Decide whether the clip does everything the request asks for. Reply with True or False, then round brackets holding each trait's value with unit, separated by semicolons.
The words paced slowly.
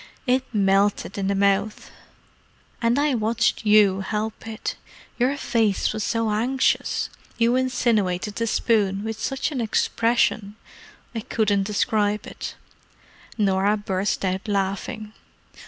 True (115 wpm)